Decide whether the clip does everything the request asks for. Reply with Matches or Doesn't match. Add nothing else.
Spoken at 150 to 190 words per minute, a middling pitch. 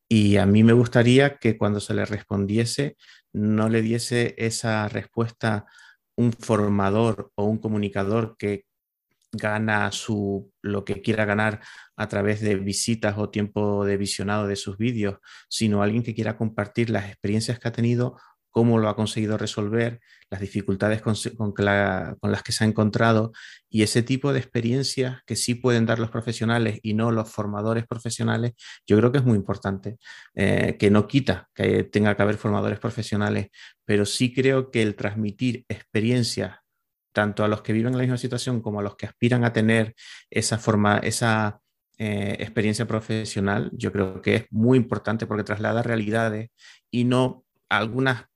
Doesn't match